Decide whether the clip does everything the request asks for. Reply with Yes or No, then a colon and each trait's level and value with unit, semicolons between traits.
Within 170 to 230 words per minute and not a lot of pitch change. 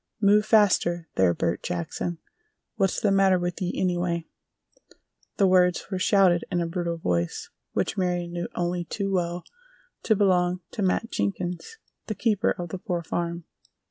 No: average, 155 wpm; narrow, 2.2 semitones